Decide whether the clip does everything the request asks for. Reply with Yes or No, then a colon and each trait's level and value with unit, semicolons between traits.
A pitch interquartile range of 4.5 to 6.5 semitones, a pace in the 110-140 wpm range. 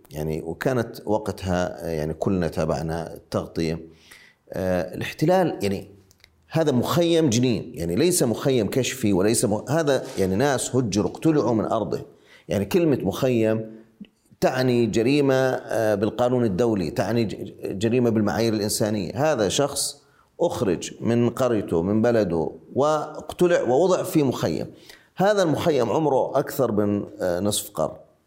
Yes: average, 5.2 semitones; average, 120 wpm